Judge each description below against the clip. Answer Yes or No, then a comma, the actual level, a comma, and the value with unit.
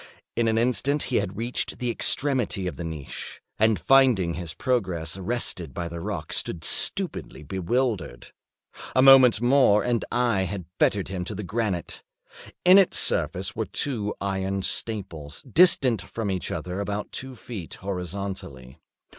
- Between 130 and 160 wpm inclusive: Yes, average, 150 wpm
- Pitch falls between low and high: No, low, 100 Hz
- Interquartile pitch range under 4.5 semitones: No, wide, 5.4 semitones